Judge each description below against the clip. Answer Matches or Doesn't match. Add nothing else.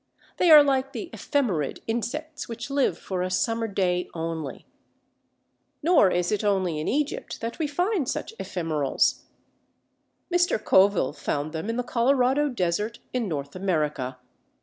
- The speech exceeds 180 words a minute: Doesn't match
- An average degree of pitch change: Doesn't match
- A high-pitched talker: Matches